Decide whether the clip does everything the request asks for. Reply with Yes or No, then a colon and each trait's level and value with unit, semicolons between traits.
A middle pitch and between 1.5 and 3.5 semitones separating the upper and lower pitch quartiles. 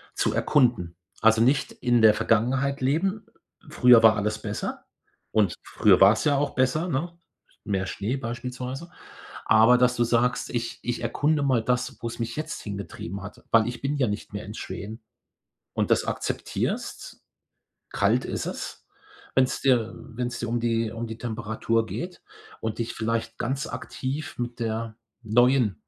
No: low, 120 Hz; average, 2.7 semitones